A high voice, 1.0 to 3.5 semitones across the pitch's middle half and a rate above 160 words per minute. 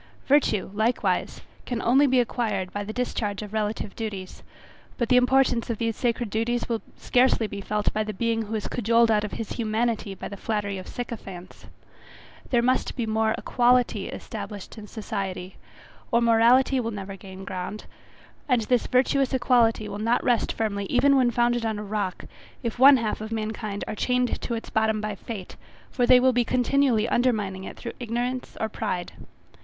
Yes: high, 225 Hz; average, 2.7 semitones; average, 180 wpm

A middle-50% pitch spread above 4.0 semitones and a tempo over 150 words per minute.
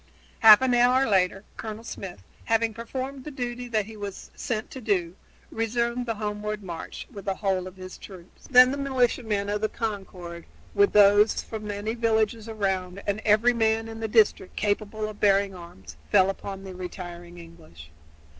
No: average, 3.0 semitones; average, 170 wpm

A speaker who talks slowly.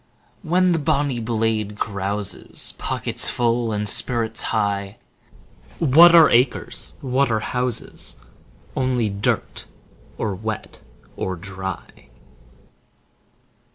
Yes: slow, 100 wpm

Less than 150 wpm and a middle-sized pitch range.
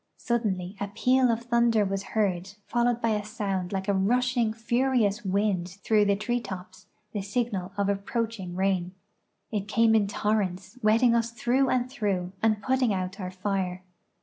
No: average, 165 wpm; average, 3.5 semitones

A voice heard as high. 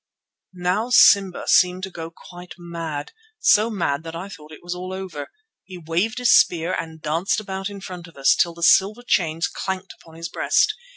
No: medium, 175 Hz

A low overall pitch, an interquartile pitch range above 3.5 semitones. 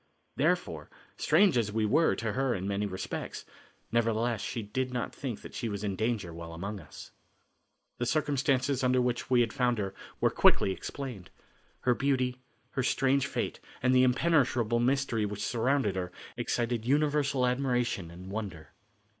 Yes: low, 120 Hz; average, 4.0 semitones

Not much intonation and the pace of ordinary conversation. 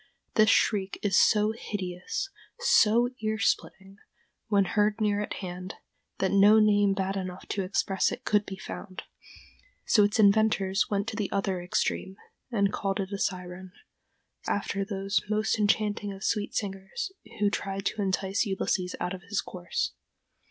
Yes: narrow, 1.6 semitones; average, 155 wpm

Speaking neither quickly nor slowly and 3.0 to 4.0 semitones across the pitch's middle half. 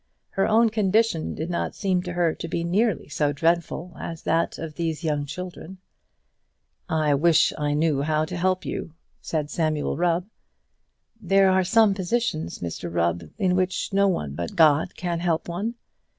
Yes: average, 170 wpm; average, 3.4 semitones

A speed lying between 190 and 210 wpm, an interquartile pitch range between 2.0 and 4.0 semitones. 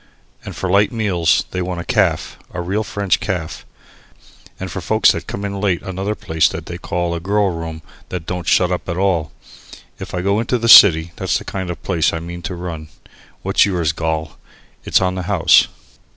Yes: fast, 205 wpm; average, 2.9 semitones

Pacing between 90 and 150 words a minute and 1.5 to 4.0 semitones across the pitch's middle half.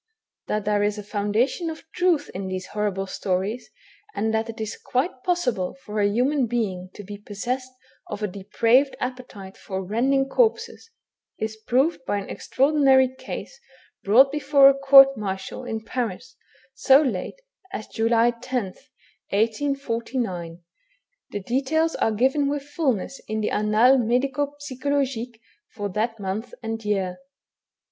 No: average, 140 wpm; average, 4.6 semitones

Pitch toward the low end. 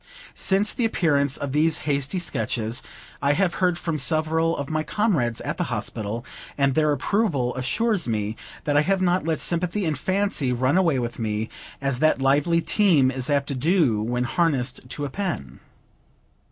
No: medium, 145 Hz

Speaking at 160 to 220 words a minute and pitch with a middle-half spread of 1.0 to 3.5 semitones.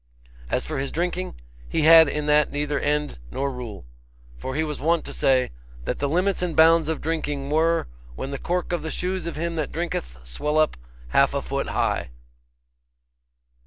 Yes: average, 185 wpm; average, 3.0 semitones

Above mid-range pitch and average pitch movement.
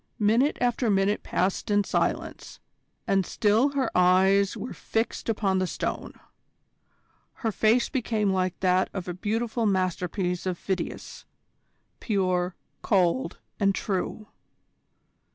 Yes: high, 195 Hz; average, 3.2 semitones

